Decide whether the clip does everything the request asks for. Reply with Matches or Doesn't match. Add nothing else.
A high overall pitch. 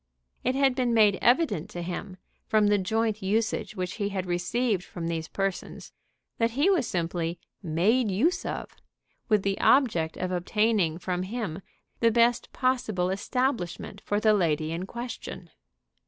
Matches